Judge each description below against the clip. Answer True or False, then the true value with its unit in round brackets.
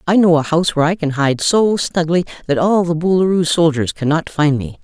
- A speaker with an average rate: False (225 wpm)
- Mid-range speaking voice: True (165 Hz)